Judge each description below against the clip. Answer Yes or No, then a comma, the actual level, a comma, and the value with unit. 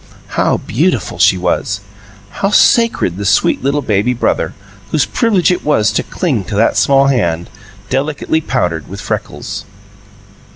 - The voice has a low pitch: Yes, low, 125 Hz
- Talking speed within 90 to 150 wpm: Yes, average, 140 wpm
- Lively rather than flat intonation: Yes, wide, 7.3 semitones